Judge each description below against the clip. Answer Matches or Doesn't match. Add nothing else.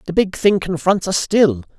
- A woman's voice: Doesn't match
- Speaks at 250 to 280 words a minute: Doesn't match